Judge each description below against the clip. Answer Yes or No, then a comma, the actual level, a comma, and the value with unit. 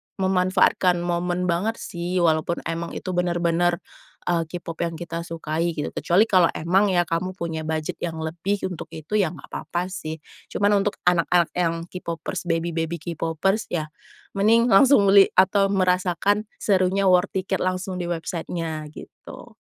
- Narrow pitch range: Yes, narrow, 2.1 semitones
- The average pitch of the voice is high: No, medium, 175 Hz